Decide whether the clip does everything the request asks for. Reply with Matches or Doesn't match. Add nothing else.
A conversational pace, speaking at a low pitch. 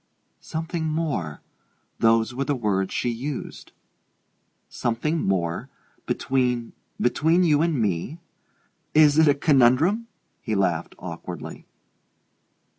Doesn't match